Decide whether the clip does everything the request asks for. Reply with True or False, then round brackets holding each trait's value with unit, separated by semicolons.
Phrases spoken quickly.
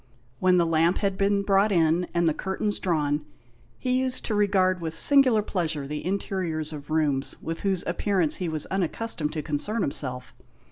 False (175 wpm)